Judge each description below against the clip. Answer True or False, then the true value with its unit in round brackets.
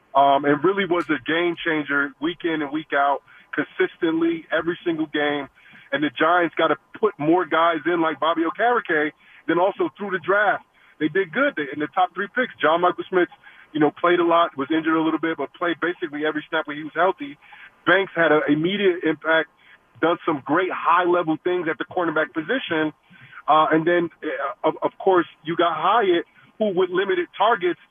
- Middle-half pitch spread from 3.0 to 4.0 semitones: True (3.7 semitones)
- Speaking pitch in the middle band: True (170 Hz)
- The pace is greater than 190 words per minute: True (200 wpm)